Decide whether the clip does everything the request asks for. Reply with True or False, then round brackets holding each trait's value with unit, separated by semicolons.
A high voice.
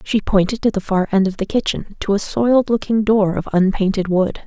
True (200 Hz)